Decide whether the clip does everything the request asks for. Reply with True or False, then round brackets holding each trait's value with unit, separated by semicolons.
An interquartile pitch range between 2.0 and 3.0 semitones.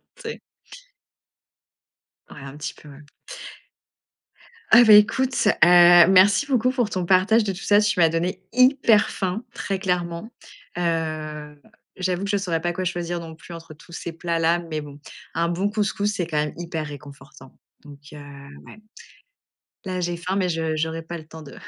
False (3.5 semitones)